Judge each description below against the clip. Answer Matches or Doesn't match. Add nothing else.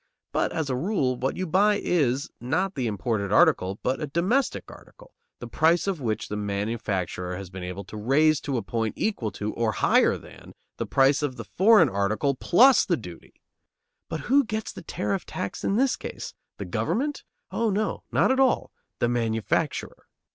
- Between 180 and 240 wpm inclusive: Matches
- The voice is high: Doesn't match